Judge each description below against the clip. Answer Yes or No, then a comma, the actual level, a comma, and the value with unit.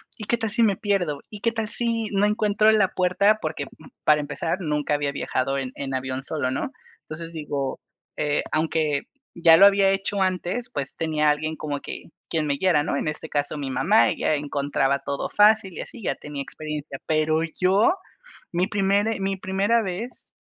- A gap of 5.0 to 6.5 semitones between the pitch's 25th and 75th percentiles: Yes, wide, 5.5 semitones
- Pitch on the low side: No, medium, 165 Hz